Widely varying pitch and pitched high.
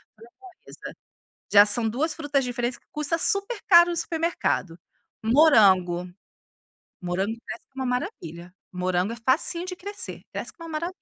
Yes: wide, 8.9 semitones; very high, 260 Hz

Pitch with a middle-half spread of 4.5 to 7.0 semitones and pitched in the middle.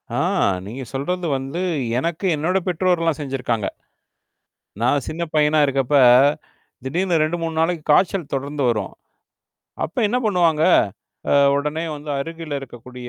No: average, 3.9 semitones; medium, 150 Hz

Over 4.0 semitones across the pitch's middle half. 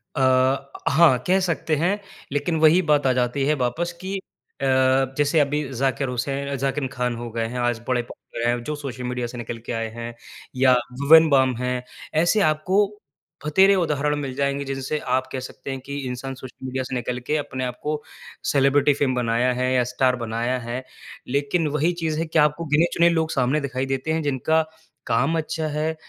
No: average, 3.3 semitones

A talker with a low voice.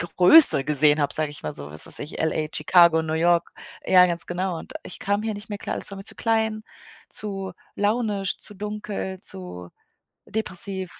No: medium, 185 Hz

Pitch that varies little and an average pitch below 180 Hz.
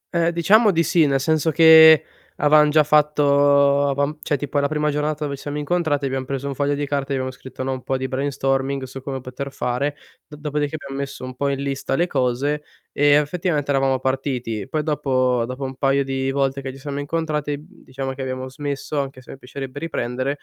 Yes: narrow, 1.9 semitones; medium, 140 Hz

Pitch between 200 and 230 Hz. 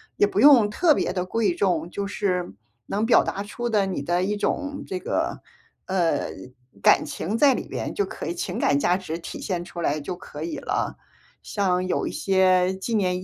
No: high, 190 Hz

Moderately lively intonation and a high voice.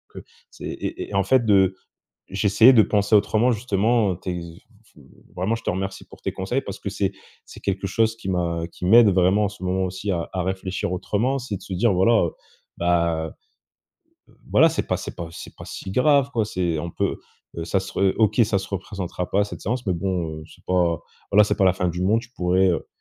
No: average, 3.0 semitones; very low, 95 Hz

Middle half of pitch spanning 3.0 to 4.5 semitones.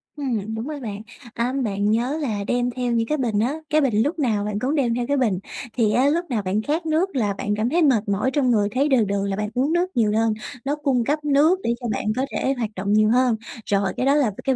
No: average, 4.9 semitones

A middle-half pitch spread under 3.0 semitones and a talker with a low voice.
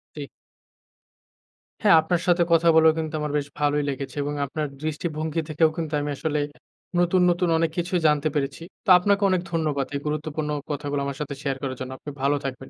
No: narrow, 2.5 semitones; medium, 150 Hz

